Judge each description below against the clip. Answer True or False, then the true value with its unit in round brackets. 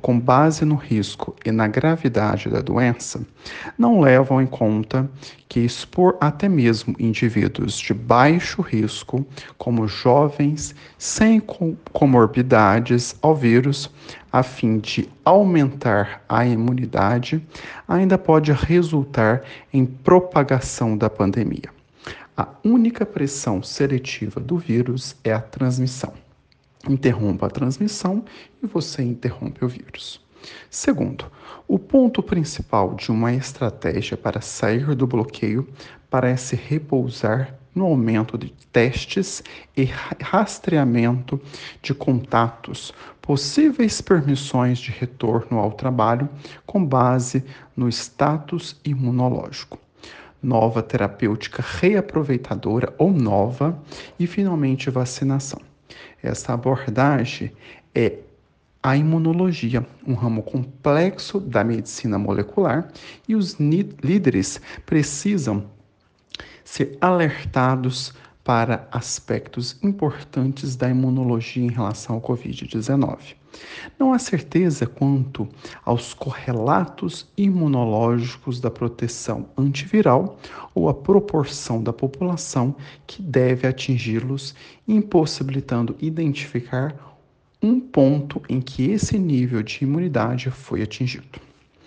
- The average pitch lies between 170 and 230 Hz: False (130 Hz)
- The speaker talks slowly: True (100 wpm)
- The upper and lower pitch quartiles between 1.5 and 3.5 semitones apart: False (4.1 semitones)